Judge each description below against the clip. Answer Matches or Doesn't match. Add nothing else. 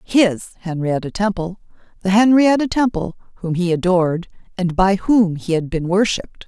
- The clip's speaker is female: Matches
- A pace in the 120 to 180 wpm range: Matches